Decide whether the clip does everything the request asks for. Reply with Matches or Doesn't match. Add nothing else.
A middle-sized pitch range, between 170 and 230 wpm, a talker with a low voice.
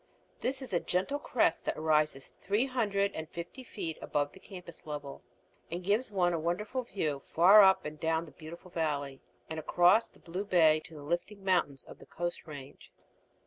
Doesn't match